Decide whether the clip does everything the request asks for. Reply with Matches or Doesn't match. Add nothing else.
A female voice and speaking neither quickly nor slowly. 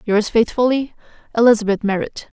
Doesn't match